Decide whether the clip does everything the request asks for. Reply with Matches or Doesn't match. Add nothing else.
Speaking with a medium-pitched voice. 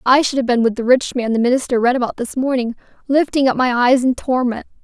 Doesn't match